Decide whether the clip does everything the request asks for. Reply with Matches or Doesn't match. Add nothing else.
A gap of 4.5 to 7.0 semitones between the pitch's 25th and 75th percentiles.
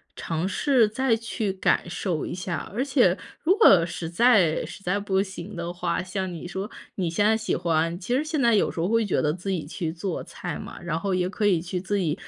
Doesn't match